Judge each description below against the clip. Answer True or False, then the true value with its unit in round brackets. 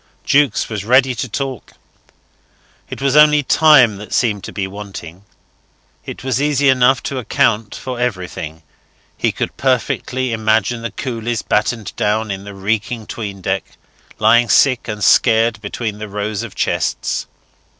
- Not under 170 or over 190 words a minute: False (150 wpm)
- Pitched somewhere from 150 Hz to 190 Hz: False (115 Hz)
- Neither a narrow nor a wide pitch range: True (3.8 semitones)